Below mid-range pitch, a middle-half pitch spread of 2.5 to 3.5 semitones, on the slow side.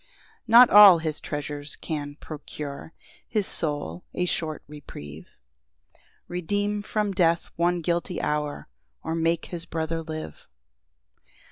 No: medium, 165 Hz; average, 3.2 semitones; slow, 125 wpm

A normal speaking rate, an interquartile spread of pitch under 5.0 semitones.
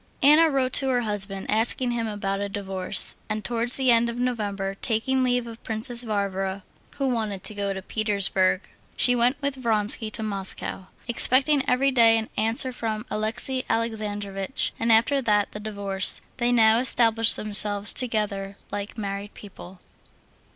Yes: average, 160 wpm; average, 3.2 semitones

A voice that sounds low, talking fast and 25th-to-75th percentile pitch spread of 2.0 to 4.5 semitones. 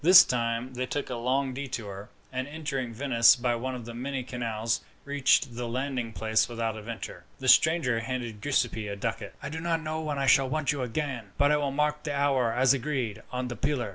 Yes: low, 130 Hz; fast, 210 wpm; average, 3.4 semitones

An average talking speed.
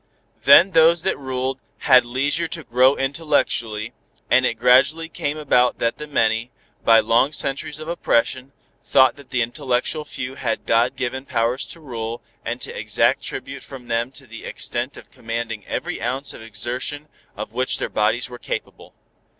Yes: average, 165 wpm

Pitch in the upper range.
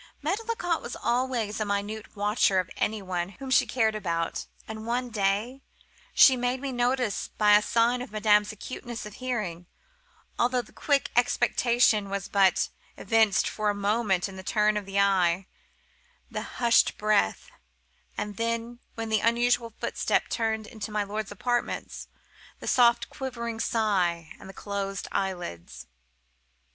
Yes: high, 215 Hz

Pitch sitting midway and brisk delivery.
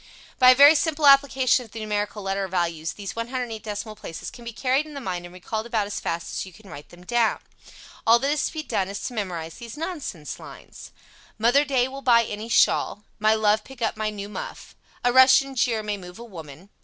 No: high, 220 Hz; fast, 225 wpm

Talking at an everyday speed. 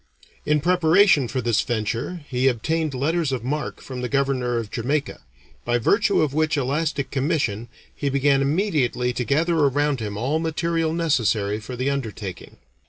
Yes: average, 160 wpm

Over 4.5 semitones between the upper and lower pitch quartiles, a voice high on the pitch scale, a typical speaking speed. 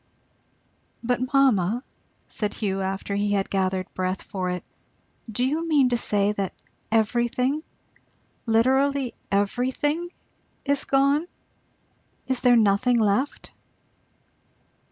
No: average, 5.1 semitones; high, 235 Hz; slow, 105 wpm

